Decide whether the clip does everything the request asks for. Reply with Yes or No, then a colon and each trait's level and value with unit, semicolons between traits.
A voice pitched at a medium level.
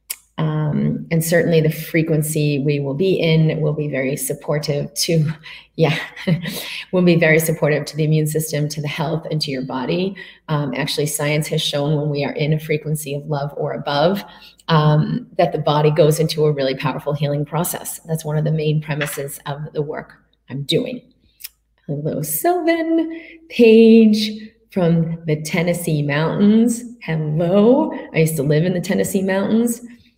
Yes: medium, 155 Hz